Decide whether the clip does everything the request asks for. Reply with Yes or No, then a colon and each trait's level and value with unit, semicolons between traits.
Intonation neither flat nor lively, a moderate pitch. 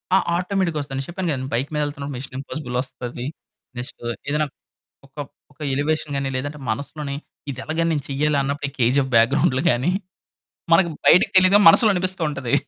Yes: average, 3.2 semitones; medium, 145 Hz